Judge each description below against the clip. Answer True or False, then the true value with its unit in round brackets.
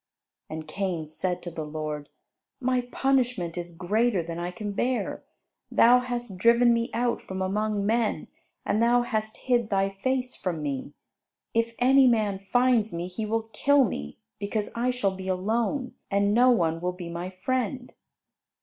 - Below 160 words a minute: False (165 wpm)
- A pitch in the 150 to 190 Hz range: False (210 Hz)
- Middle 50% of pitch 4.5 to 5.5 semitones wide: True (5.1 semitones)